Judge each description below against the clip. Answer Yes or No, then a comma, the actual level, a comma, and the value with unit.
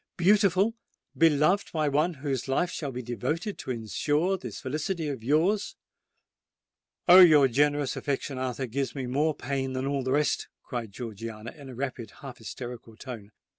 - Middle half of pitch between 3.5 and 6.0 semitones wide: Yes, average, 4.0 semitones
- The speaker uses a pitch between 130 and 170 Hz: Yes, medium, 140 Hz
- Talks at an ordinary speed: Yes, average, 150 wpm